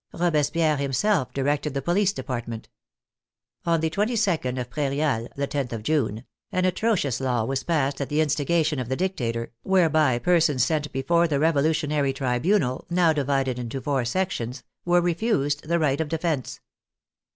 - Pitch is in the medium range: Yes, medium, 145 Hz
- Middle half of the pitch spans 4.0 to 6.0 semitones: Yes, average, 4.3 semitones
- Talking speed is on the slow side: No, average, 150 wpm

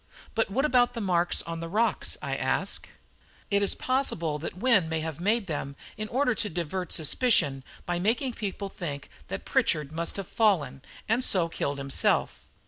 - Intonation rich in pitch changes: Yes, wide, 5.8 semitones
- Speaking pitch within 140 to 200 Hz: Yes, medium, 185 Hz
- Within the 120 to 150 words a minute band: No, average, 175 wpm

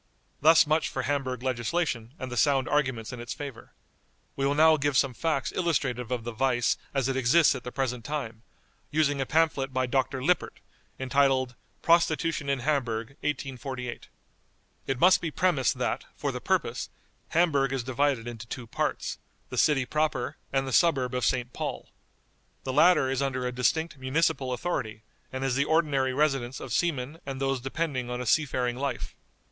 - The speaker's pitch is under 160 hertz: Yes, low, 135 Hz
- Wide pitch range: No, average, 3.0 semitones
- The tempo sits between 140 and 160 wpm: No, average, 175 wpm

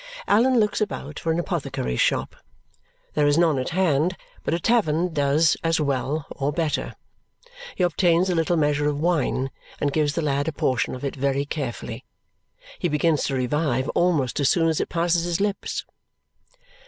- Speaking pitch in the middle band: Yes, medium, 155 Hz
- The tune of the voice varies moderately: Yes, average, 3.5 semitones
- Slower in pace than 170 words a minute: No, average, 175 wpm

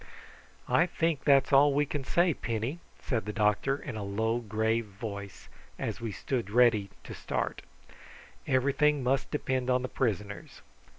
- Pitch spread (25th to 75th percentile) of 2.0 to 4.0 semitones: No, average, 4.4 semitones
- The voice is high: No, low, 120 Hz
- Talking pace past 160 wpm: No, average, 155 wpm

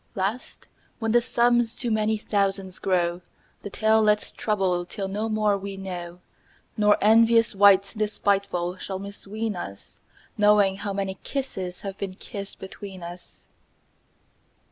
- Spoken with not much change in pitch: Yes, narrow, 2.1 semitones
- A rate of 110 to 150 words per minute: Yes, average, 140 wpm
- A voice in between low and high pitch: No, high, 200 Hz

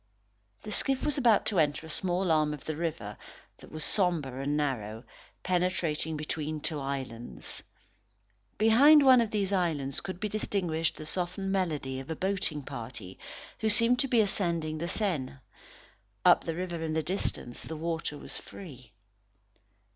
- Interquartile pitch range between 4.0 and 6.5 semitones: Yes, average, 4.8 semitones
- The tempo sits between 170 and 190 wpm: No, average, 160 wpm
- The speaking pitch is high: No, medium, 160 Hz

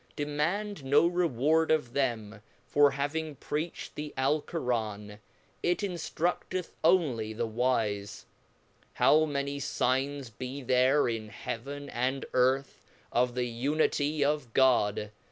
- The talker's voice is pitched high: No, medium, 140 Hz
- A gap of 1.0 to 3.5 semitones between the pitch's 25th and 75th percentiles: No, average, 4.0 semitones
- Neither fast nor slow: No, slow, 115 wpm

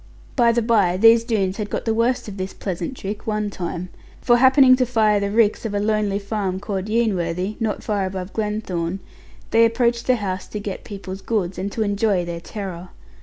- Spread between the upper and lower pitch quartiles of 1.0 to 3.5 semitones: Yes, average, 3.1 semitones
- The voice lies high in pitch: Yes, high, 205 Hz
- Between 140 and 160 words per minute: No, average, 200 wpm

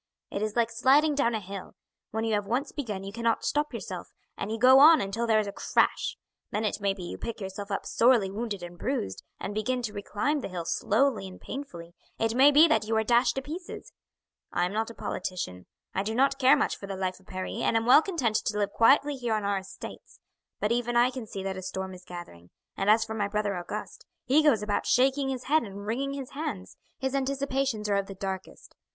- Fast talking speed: Yes, fast, 235 wpm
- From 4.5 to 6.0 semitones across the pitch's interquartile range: Yes, average, 4.9 semitones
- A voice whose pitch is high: Yes, high, 220 Hz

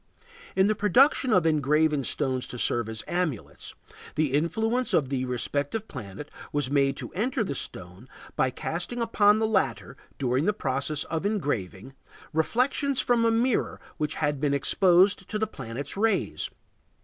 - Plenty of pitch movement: Yes, wide, 8.0 semitones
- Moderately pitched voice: Yes, medium, 155 Hz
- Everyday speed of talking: Yes, average, 155 wpm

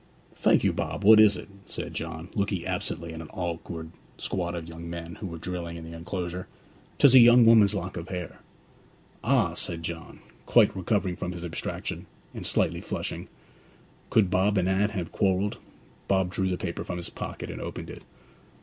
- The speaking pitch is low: Yes, very low, 90 Hz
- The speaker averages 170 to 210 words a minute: Yes, average, 185 wpm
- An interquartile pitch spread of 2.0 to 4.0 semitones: Yes, average, 2.7 semitones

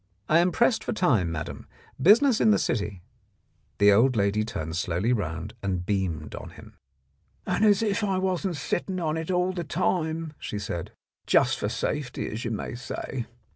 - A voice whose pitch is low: Yes, low, 130 Hz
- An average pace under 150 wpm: No, average, 175 wpm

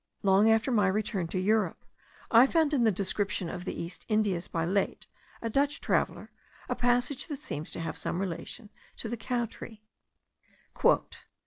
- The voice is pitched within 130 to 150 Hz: No, high, 215 Hz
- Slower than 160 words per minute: No, average, 170 wpm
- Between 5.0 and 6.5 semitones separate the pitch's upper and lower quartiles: No, average, 4.2 semitones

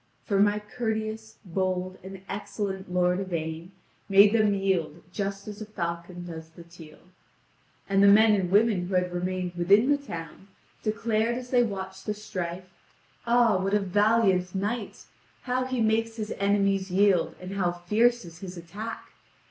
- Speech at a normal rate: Yes, average, 160 wpm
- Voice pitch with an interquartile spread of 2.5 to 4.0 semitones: Yes, average, 3.1 semitones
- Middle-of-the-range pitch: No, high, 195 Hz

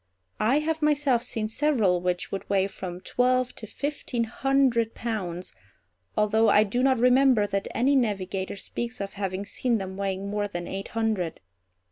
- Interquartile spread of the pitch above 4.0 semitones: Yes, average, 4.4 semitones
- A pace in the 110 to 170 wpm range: Yes, average, 160 wpm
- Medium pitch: No, high, 220 Hz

